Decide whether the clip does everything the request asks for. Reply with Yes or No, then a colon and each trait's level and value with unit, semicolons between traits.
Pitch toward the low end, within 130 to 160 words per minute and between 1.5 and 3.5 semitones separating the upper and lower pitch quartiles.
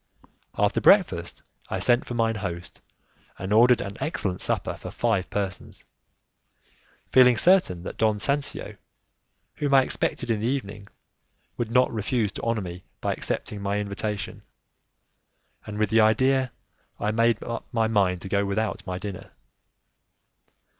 Yes: low, 110 Hz; average, 145 wpm; average, 3.2 semitones